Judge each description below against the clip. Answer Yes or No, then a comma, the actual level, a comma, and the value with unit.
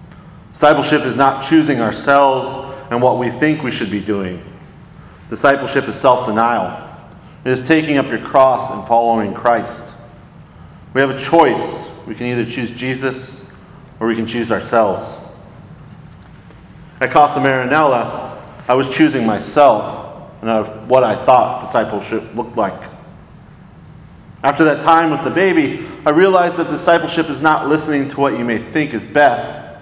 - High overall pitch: No, low, 135 Hz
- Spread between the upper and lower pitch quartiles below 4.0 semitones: No, average, 4.6 semitones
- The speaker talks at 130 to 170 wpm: Yes, average, 150 wpm